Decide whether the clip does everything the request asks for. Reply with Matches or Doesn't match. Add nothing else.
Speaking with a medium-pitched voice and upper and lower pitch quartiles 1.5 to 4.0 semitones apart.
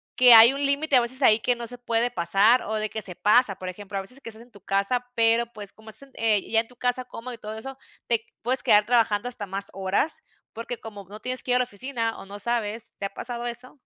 Doesn't match